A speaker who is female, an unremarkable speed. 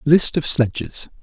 No: male; average, 145 wpm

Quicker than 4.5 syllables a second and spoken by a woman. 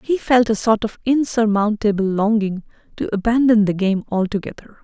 Yes: 5.2 syllables/s; female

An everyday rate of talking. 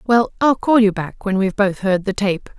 No: fast, 255 wpm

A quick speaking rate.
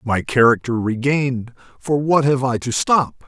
No: average, 165 wpm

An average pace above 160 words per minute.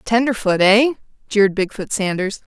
No: average, 140 wpm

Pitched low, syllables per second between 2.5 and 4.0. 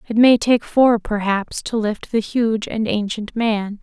No: high, 220 Hz; 3.8 syllables/s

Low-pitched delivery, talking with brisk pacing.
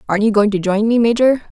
No: high, 220 Hz; fast, 265 wpm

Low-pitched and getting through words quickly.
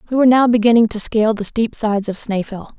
No: high, 220 Hz; fast, 235 wpm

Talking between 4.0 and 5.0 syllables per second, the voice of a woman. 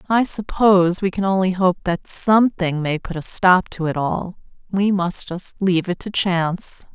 Yes: 4.7 syllables/s; female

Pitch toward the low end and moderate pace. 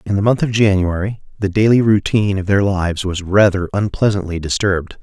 Yes: low, 100 Hz; average, 180 wpm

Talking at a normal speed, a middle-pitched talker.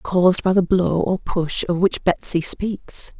Yes: average, 190 wpm; medium, 180 Hz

